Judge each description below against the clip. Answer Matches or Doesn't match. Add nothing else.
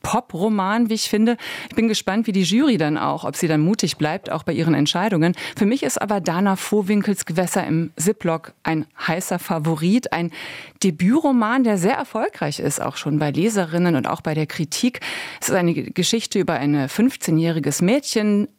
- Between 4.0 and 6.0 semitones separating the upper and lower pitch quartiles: Matches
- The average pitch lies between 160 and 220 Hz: Matches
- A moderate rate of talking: Matches